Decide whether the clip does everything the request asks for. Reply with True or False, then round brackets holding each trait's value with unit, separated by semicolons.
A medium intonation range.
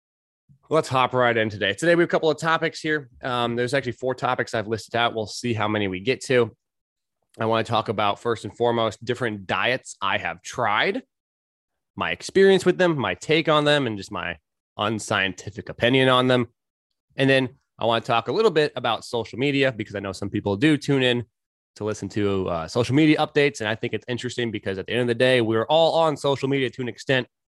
True (4.3 semitones)